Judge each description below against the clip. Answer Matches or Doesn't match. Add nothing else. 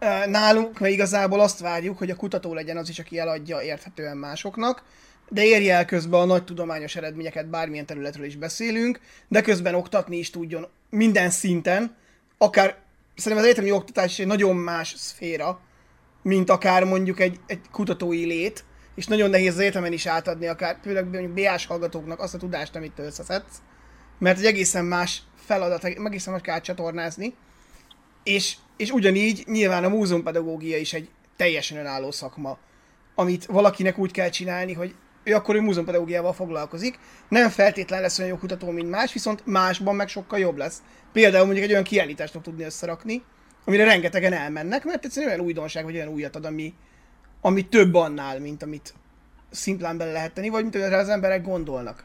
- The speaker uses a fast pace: Matches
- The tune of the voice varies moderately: Matches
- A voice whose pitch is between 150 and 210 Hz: Matches